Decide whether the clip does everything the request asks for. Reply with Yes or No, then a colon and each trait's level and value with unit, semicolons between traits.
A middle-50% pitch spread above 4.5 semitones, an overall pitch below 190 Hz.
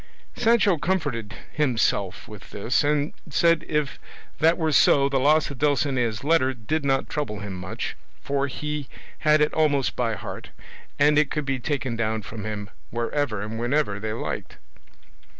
Yes: average, 5.0 semitones; medium, 140 Hz